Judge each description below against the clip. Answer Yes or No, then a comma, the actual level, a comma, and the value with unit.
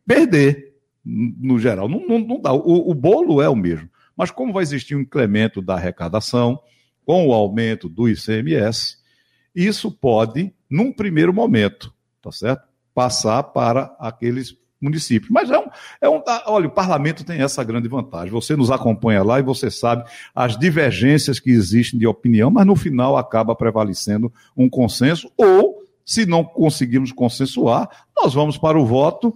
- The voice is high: No, low, 130 Hz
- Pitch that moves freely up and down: Yes, wide, 6.0 semitones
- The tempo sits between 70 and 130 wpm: No, average, 160 wpm